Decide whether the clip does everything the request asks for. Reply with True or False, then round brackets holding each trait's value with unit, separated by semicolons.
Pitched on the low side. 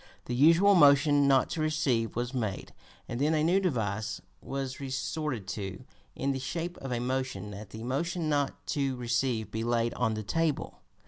True (130 Hz)